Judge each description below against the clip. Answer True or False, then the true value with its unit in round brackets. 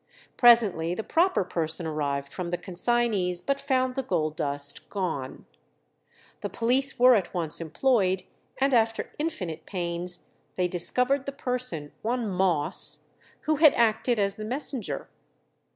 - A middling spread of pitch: False (6.6 semitones)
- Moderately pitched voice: False (200 Hz)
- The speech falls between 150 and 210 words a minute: False (135 wpm)